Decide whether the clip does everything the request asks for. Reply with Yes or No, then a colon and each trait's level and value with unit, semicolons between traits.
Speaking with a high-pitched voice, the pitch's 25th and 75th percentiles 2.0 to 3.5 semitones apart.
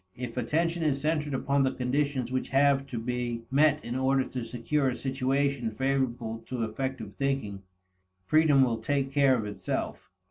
No: low, 130 Hz; average, 2.7 semitones